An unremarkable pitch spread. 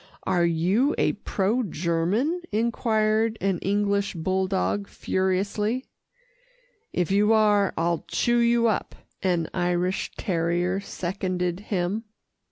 Yes: average, 3.4 semitones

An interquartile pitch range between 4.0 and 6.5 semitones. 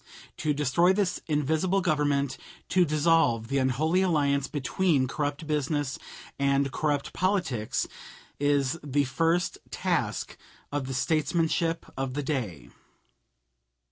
No: average, 3.1 semitones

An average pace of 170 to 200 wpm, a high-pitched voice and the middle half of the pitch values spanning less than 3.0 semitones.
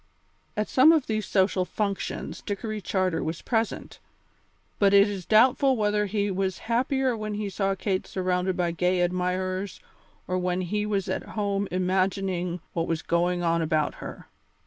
No: average, 160 wpm; high, 195 Hz; narrow, 2.6 semitones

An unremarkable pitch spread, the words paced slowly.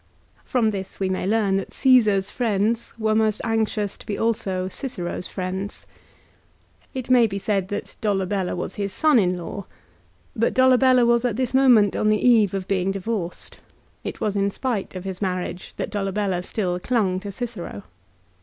No: average, 3.4 semitones; average, 175 wpm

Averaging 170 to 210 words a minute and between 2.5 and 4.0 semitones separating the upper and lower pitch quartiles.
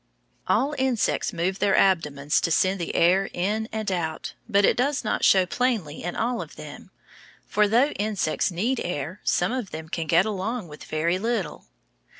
No: average, 175 wpm; average, 4.6 semitones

